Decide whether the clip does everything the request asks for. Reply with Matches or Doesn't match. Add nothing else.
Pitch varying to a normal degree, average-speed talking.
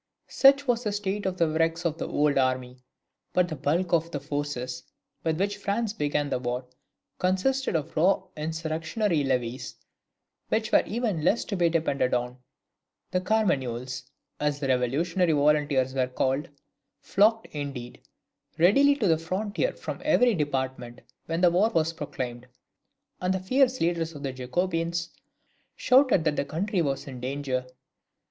Doesn't match